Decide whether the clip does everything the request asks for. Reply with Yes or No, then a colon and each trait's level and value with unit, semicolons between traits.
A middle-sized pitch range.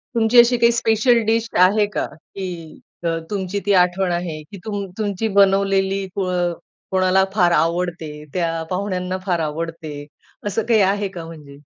Yes: average, 3.1 semitones